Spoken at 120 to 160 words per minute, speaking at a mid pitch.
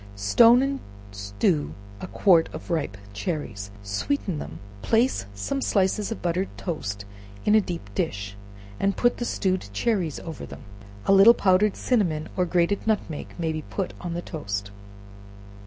Yes: average, 155 wpm; medium, 175 Hz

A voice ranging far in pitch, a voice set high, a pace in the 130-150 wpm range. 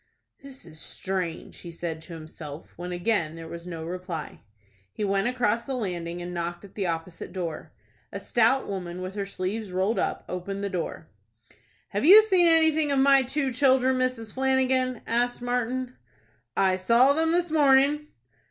No: wide, 6.8 semitones; high, 210 Hz; average, 170 wpm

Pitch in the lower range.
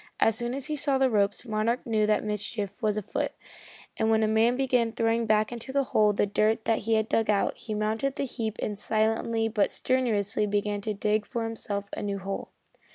No: high, 220 Hz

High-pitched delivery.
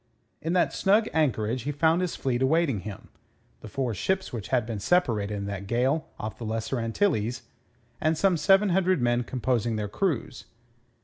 No: low, 130 Hz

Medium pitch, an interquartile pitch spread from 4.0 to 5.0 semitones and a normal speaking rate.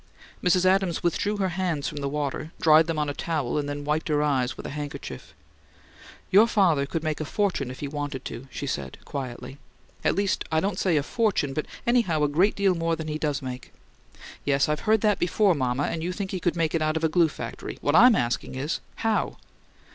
No: medium, 155 Hz; average, 4.3 semitones; fast, 225 wpm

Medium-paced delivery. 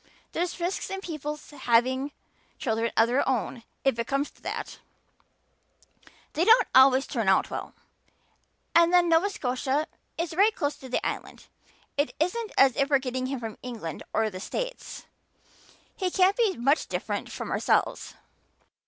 Yes: average, 160 wpm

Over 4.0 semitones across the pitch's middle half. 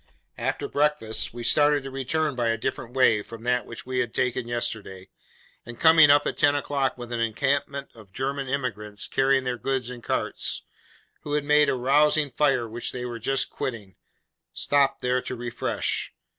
No: average, 3.1 semitones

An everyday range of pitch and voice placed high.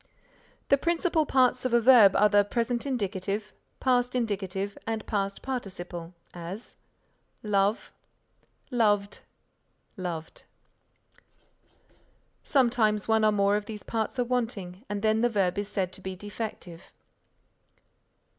Yes: average, 3.5 semitones; high, 210 Hz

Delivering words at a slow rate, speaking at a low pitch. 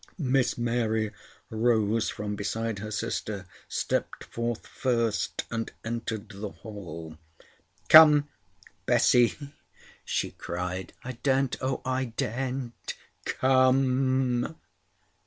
Yes: slow, 95 wpm; low, 115 Hz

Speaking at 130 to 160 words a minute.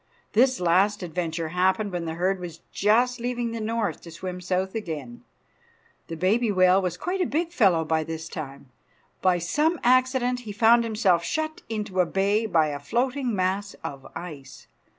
No: average, 170 wpm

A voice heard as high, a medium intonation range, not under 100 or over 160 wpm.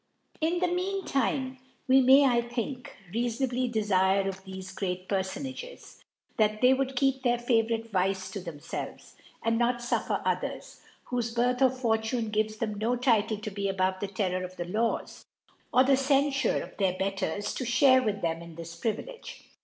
No: high, 230 Hz; average, 4.9 semitones; average, 175 wpm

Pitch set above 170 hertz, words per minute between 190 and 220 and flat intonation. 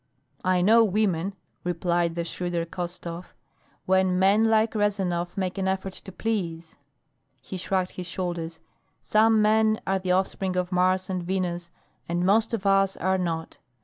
No: medium, 185 Hz; average, 155 wpm; narrow, 2.0 semitones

